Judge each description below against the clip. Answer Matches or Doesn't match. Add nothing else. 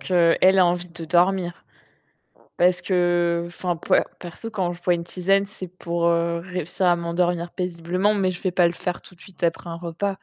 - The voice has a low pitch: Doesn't match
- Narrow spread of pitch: Matches